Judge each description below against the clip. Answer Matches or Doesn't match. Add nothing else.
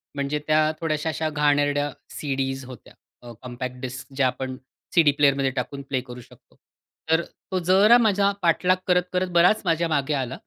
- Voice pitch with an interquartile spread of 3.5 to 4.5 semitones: Matches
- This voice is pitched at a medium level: Matches